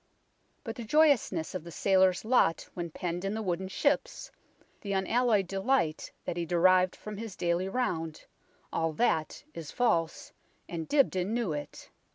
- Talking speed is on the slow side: No, average, 155 wpm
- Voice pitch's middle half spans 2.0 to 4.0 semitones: No, average, 4.9 semitones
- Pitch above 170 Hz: Yes, medium, 185 Hz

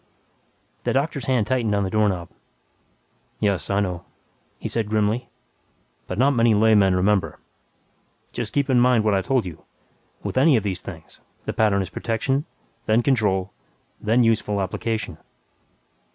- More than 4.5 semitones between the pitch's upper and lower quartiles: No, average, 3.6 semitones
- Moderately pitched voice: No, low, 110 Hz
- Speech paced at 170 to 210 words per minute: No, average, 150 wpm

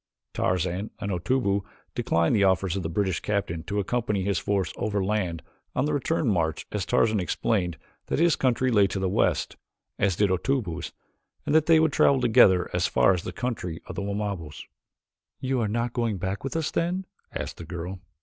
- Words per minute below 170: No, average, 190 wpm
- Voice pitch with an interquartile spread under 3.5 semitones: No, average, 4.9 semitones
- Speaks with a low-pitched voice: Yes, low, 100 Hz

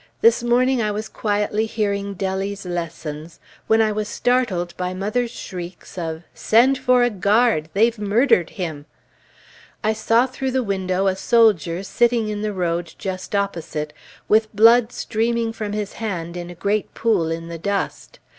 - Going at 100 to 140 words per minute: No, average, 160 wpm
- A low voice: No, high, 205 Hz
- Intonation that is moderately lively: Yes, average, 4.2 semitones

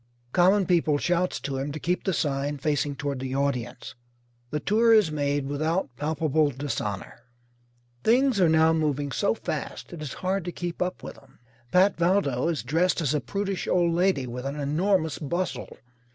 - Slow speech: No, average, 175 wpm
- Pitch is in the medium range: Yes, medium, 155 Hz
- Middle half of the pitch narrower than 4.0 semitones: No, average, 4.3 semitones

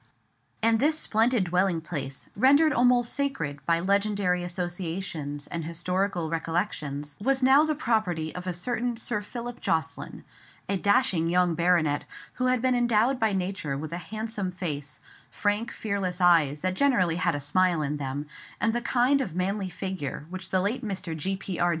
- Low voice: No, medium, 185 Hz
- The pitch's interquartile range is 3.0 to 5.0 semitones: No, wide, 5.4 semitones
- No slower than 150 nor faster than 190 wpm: Yes, average, 160 wpm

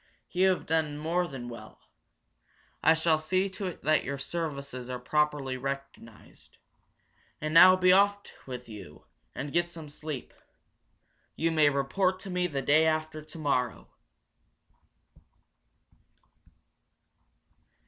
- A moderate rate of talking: No, slow, 120 wpm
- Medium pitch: Yes, medium, 155 Hz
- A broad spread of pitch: No, average, 3.9 semitones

